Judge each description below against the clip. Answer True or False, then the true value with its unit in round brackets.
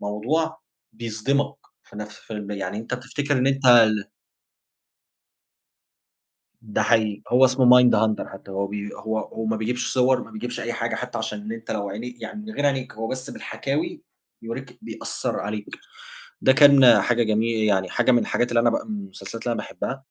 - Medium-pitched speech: False (115 Hz)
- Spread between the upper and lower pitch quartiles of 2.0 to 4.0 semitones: True (3.1 semitones)